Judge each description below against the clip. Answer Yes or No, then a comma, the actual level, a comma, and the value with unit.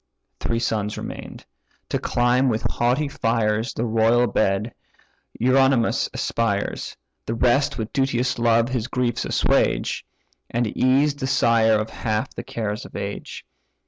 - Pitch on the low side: Yes, low, 115 Hz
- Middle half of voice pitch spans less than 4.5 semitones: Yes, narrow, 2.5 semitones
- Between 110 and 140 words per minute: Yes, slow, 135 wpm